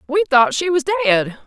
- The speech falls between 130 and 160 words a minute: No, fast, 205 wpm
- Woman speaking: Yes, female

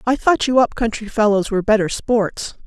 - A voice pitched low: No, high, 225 Hz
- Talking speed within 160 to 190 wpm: No, fast, 205 wpm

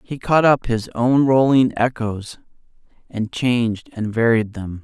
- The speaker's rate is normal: Yes, average, 150 wpm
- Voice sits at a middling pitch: No, low, 115 Hz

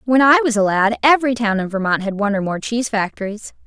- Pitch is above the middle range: Yes, high, 225 Hz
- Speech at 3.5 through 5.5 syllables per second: No, 6.4 syllables/s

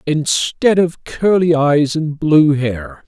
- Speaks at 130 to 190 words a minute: Yes, slow, 135 wpm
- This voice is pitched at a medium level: Yes, medium, 150 Hz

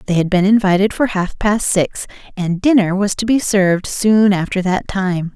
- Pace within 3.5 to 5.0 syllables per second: Yes, 4.7 syllables/s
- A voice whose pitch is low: No, high, 195 Hz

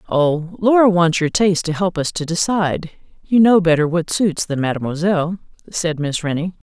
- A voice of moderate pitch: Yes, medium, 170 Hz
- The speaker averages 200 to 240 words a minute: No, average, 180 wpm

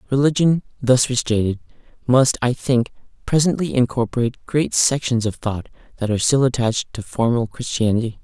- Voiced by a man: Yes, male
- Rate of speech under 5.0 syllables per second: No, 5.5 syllables/s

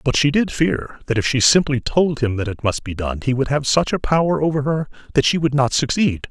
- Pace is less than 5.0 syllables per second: No, 5.5 syllables/s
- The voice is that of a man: Yes, male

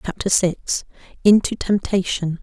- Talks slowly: Yes, slow, 100 wpm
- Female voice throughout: Yes, female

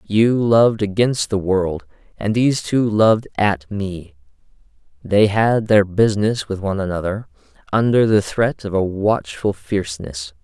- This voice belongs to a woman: No, male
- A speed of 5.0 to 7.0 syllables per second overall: No, 4.4 syllables/s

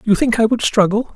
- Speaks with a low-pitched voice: No, high, 220 Hz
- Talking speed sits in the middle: No, fast, 260 wpm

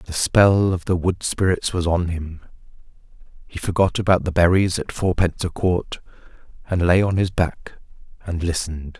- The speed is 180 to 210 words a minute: No, average, 165 wpm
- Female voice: No, male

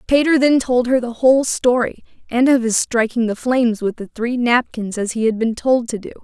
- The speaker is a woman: Yes, female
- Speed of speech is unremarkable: No, fast, 230 wpm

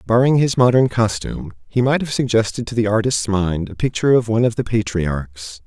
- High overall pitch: No, low, 115 Hz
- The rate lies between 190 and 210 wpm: Yes, average, 200 wpm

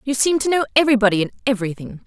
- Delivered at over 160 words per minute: Yes, fast, 205 wpm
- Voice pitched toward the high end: Yes, high, 240 Hz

